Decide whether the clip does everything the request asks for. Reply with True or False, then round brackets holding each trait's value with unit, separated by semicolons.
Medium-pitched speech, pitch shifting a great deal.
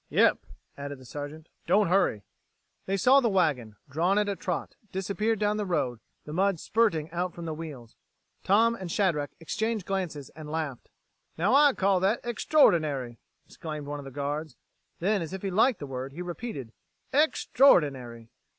True (170 Hz; 5.8 semitones)